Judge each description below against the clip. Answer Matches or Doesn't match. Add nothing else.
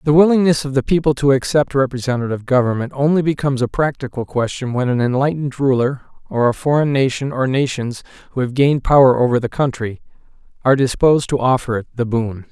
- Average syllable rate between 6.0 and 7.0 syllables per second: Matches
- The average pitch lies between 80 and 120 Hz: Doesn't match